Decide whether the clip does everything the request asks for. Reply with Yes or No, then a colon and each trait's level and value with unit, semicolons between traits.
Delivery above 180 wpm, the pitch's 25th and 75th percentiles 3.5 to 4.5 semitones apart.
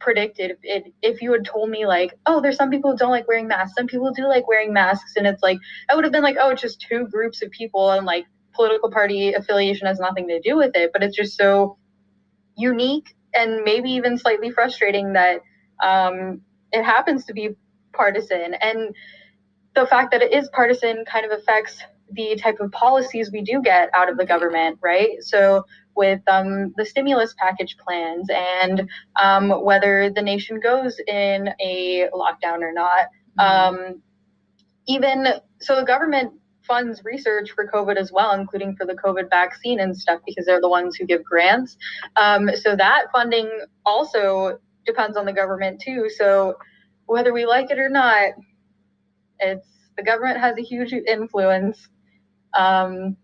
No: average, 175 wpm; average, 3.9 semitones